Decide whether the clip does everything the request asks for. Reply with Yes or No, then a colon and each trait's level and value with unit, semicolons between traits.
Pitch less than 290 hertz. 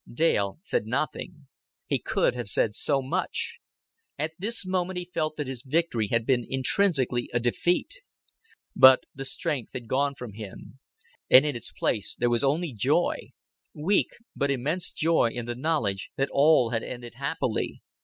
Yes: low, 135 Hz